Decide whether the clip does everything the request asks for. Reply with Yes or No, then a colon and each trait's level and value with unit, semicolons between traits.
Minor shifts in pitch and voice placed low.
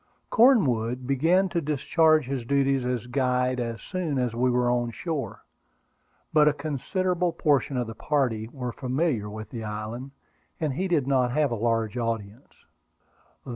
No: average, 4.2 semitones; low, 130 Hz